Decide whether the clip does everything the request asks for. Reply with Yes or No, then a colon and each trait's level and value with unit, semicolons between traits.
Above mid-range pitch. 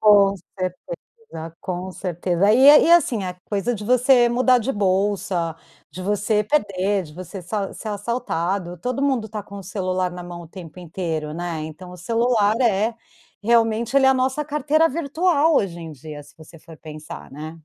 Yes: high, 200 Hz